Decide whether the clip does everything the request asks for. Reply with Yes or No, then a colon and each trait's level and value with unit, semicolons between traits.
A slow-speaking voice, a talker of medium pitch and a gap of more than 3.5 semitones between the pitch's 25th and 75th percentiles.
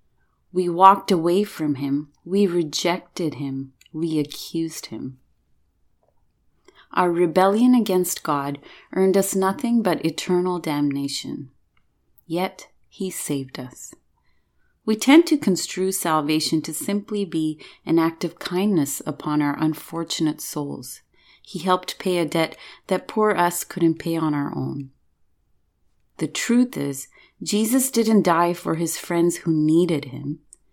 Yes: slow, 130 wpm; medium, 165 Hz; average, 4.7 semitones